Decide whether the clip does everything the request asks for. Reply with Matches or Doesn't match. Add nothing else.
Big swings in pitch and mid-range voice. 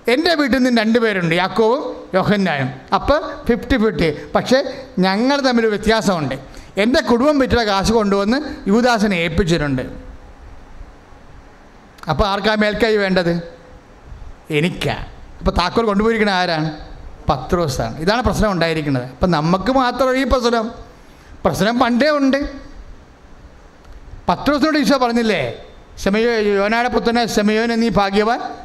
Doesn't match